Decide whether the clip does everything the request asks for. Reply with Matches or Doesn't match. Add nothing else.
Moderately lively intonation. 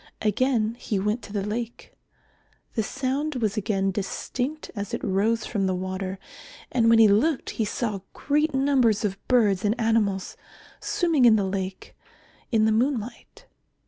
Matches